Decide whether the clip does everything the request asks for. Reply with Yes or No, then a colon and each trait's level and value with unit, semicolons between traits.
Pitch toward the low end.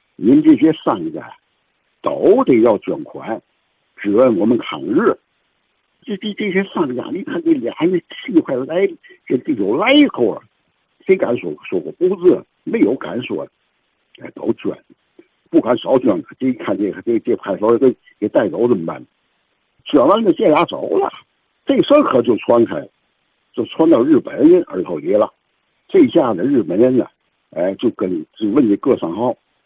No: very high, 325 Hz